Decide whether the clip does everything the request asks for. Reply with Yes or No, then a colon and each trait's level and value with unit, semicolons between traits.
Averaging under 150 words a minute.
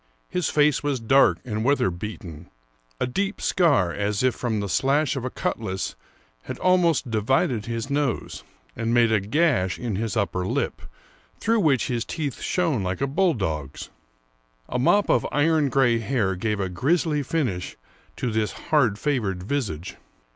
No: average, 160 wpm